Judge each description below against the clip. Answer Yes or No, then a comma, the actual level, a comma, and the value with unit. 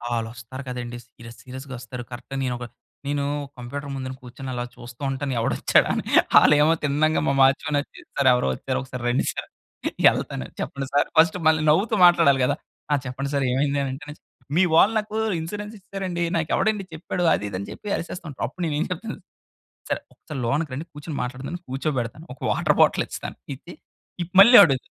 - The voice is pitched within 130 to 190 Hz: Yes, medium, 140 Hz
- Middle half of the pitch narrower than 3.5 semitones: No, average, 4.2 semitones